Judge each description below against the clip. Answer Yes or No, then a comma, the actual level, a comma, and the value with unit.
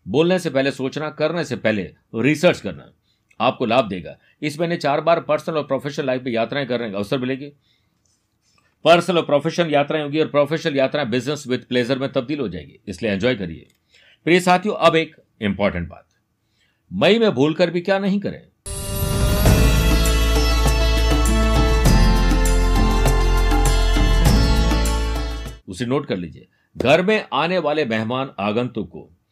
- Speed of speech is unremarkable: Yes, average, 140 wpm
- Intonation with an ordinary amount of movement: No, wide, 8.0 semitones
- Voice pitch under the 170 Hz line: Yes, low, 135 Hz